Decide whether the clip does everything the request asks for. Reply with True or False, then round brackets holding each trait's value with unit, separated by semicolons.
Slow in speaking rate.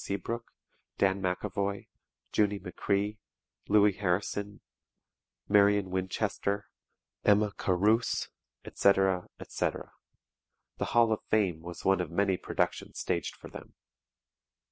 True (100 wpm)